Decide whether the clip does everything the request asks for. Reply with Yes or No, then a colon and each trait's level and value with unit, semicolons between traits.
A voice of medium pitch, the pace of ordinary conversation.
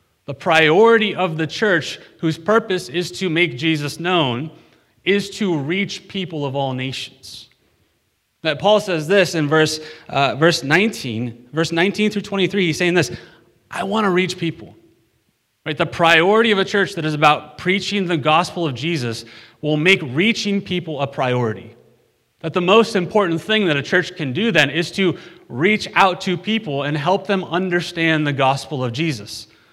Yes: medium, 165 Hz; average, 170 wpm